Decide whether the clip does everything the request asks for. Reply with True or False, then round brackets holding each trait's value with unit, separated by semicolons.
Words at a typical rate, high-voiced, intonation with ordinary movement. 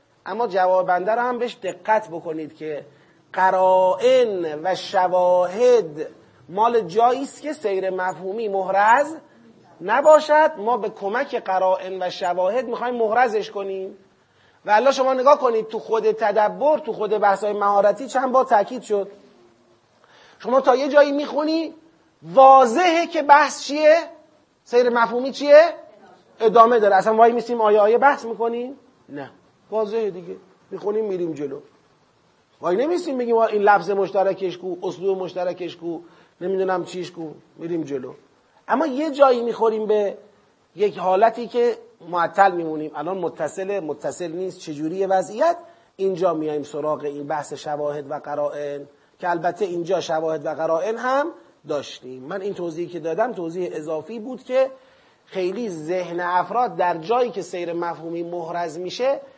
False (140 wpm; 200 Hz; 5.9 semitones)